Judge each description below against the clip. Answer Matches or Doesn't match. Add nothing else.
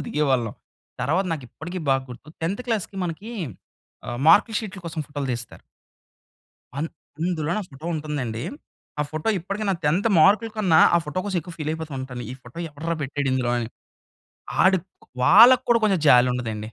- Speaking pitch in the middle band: Matches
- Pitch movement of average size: Doesn't match